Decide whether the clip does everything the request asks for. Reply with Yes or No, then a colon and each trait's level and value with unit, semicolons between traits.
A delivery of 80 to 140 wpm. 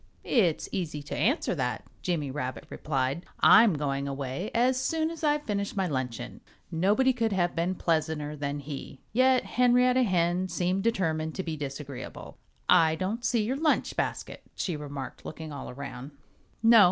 No: average, 160 wpm